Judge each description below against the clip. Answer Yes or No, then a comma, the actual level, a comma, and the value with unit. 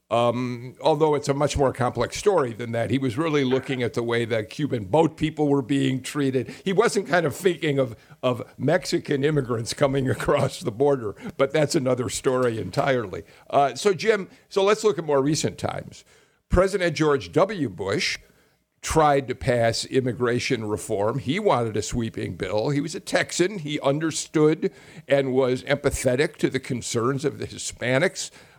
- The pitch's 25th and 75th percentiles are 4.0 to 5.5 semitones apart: No, average, 3.5 semitones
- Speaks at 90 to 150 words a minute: No, average, 170 wpm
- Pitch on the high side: No, medium, 140 Hz